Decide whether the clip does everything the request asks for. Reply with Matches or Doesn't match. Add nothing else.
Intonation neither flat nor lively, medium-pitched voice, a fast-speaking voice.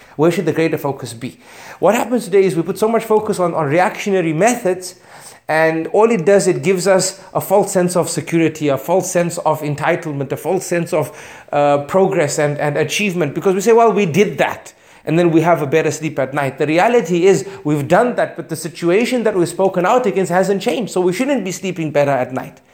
Matches